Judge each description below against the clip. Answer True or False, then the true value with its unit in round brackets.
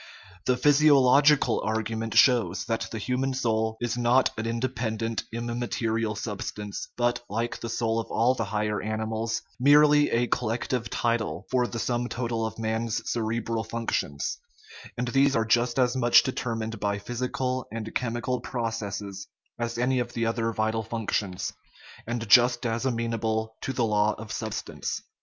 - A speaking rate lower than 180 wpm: True (155 wpm)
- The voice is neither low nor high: False (115 Hz)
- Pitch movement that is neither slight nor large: False (1.8 semitones)